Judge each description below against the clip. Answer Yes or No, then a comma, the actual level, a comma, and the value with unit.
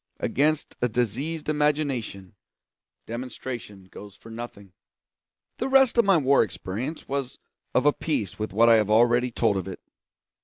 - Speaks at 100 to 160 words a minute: Yes, average, 150 wpm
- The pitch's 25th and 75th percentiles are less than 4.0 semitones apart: No, wide, 5.6 semitones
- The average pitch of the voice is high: No, low, 120 Hz